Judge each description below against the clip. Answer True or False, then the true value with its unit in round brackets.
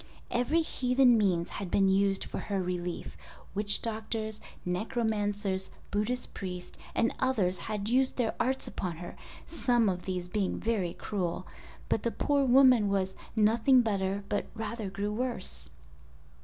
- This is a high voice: True (210 Hz)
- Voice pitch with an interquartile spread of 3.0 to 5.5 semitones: True (3.9 semitones)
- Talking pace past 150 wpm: False (140 wpm)